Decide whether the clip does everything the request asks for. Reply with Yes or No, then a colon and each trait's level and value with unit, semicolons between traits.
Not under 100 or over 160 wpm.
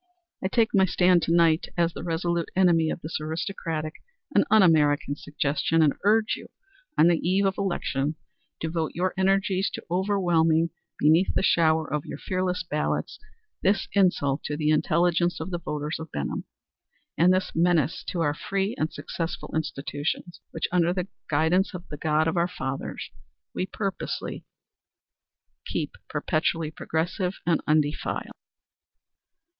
Yes: average, 150 wpm